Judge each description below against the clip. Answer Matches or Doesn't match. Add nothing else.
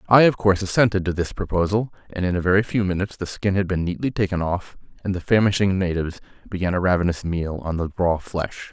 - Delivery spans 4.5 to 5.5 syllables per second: Doesn't match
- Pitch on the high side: Doesn't match